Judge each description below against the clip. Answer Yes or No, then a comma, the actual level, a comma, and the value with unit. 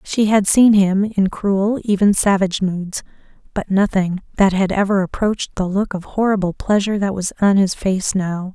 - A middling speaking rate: Yes, average, 185 wpm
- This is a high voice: Yes, high, 195 Hz